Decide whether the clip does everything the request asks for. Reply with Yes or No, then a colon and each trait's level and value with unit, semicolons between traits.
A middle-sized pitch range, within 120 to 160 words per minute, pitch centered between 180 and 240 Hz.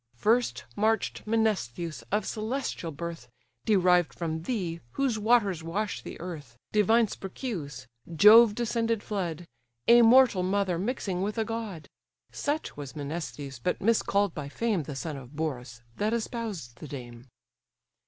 No: wide, 6.3 semitones; slow, 135 wpm; high, 190 Hz